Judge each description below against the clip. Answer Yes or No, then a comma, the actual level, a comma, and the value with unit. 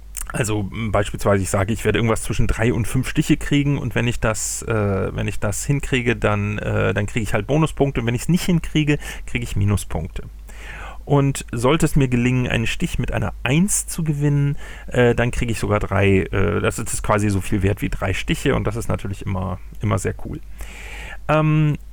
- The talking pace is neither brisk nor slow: No, fast, 205 wpm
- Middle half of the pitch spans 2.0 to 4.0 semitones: No, average, 5.3 semitones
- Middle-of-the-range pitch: No, low, 115 Hz